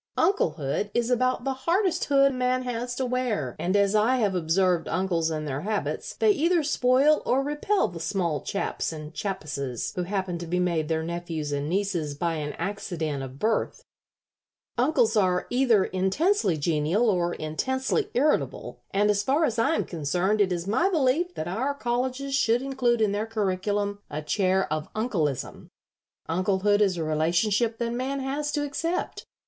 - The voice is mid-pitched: No, high, 205 Hz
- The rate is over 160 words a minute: Yes, average, 170 wpm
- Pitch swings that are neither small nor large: No, wide, 7.0 semitones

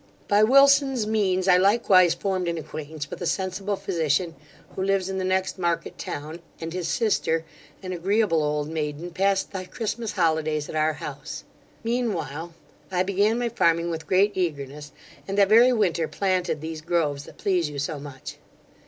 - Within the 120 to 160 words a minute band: No, average, 170 wpm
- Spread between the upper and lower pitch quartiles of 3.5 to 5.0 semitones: Yes, average, 4.0 semitones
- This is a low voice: No, medium, 180 Hz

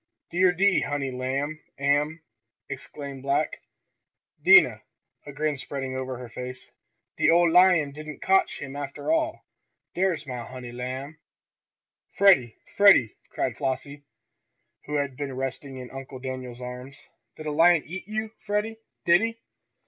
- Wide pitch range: No, average, 4.8 semitones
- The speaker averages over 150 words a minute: No, average, 140 wpm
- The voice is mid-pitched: Yes, medium, 145 Hz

